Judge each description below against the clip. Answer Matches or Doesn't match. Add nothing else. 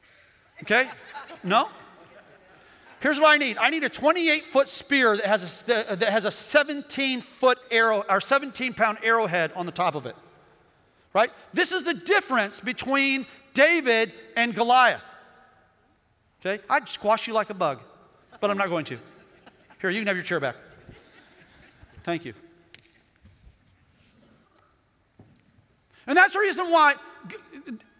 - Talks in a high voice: Matches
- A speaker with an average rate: Doesn't match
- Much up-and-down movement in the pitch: Matches